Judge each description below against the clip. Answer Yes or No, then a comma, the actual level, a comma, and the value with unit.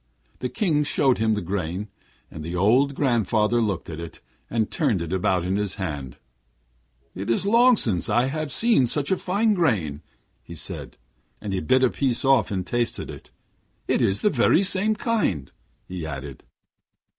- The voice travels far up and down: Yes, wide, 7.8 semitones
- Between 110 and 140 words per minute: No, average, 170 wpm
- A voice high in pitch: No, low, 110 Hz